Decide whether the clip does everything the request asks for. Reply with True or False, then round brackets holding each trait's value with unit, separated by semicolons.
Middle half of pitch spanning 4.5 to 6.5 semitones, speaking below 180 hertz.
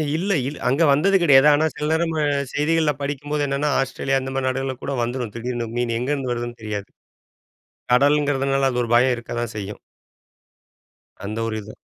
False (3.4 semitones; 135 Hz)